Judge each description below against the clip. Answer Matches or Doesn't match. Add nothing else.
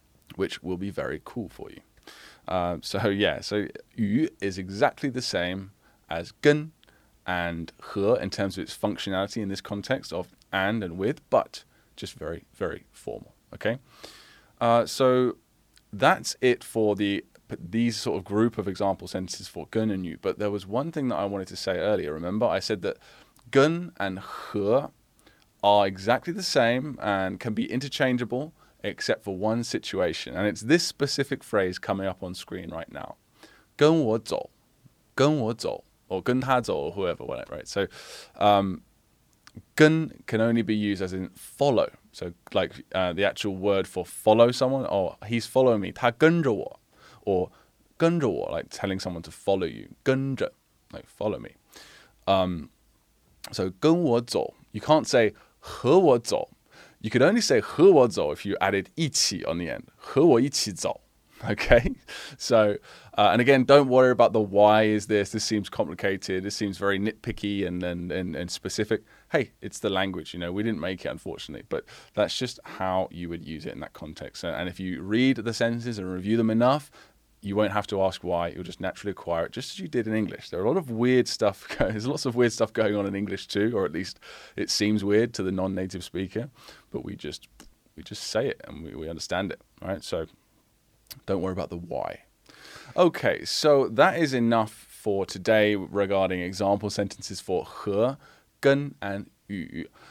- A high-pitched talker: Doesn't match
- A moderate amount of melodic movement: Matches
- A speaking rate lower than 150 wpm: Doesn't match